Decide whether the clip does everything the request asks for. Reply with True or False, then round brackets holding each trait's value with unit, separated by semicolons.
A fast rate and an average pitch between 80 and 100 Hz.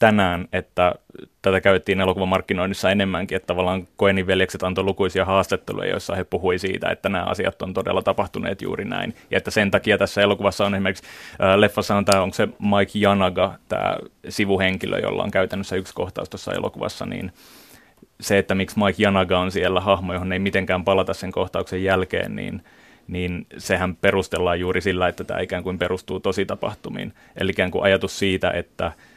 True (175 wpm; 95 Hz)